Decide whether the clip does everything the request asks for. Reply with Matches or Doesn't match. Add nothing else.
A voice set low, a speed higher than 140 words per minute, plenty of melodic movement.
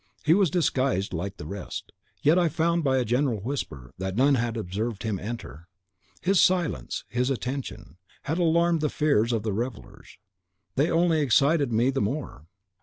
Matches